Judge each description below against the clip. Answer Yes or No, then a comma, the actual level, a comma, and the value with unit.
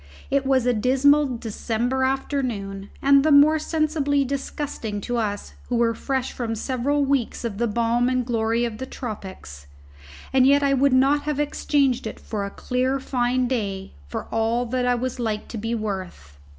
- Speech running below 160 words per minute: No, average, 175 wpm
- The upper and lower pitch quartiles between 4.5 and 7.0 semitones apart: No, average, 3.4 semitones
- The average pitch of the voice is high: Yes, very high, 250 Hz